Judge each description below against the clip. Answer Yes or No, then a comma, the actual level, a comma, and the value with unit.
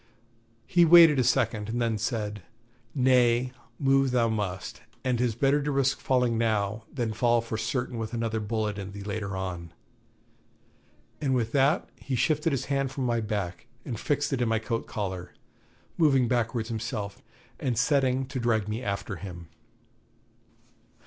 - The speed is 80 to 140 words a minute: No, average, 160 wpm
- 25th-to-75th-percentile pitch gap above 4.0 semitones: No, average, 3.5 semitones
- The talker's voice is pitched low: Yes, low, 115 Hz